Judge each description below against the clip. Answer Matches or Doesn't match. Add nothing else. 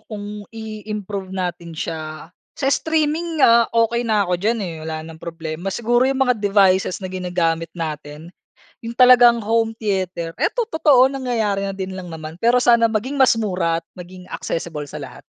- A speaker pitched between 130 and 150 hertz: Doesn't match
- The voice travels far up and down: Matches